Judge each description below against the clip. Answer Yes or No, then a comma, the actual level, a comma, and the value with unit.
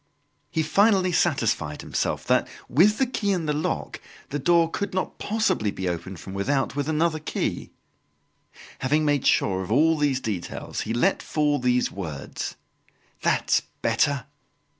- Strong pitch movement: Yes, wide, 7.0 semitones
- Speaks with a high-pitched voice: No, medium, 145 Hz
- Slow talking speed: No, average, 150 wpm